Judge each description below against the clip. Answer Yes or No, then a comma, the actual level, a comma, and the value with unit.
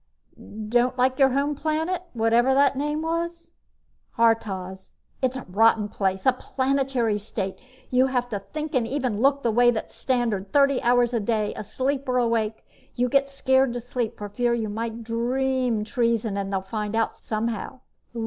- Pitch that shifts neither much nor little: Yes, average, 3.3 semitones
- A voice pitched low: No, high, 240 Hz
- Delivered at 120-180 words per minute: Yes, average, 170 wpm